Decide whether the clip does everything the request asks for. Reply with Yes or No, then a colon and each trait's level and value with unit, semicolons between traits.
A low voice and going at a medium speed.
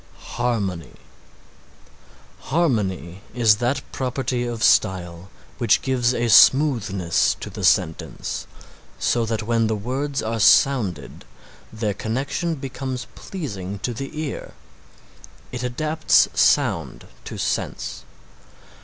No: low, 120 Hz; slow, 105 wpm